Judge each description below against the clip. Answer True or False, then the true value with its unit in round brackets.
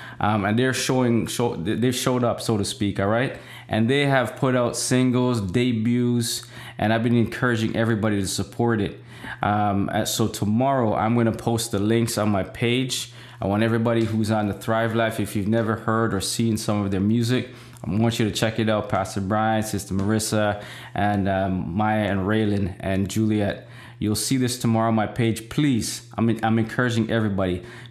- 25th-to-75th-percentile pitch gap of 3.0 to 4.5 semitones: False (2.4 semitones)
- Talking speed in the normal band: True (190 wpm)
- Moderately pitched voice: False (115 Hz)